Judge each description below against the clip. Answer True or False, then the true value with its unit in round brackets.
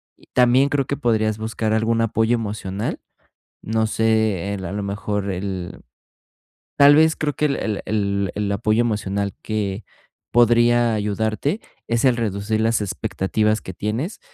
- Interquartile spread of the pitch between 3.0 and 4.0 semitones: False (2.6 semitones)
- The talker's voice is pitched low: True (110 Hz)